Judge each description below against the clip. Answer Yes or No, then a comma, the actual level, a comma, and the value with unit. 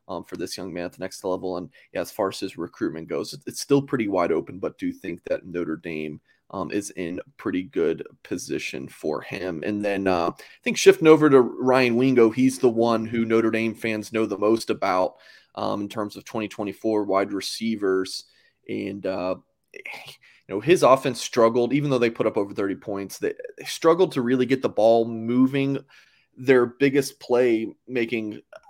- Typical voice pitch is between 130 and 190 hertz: No, low, 115 Hz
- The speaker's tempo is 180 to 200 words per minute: Yes, average, 195 wpm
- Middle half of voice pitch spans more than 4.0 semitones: Yes, average, 4.6 semitones